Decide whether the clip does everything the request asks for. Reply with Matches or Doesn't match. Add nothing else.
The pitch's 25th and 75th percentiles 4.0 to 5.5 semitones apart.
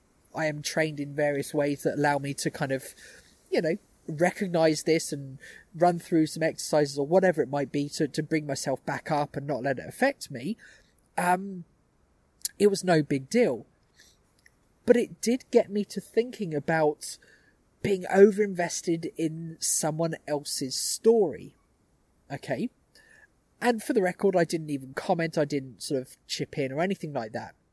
Matches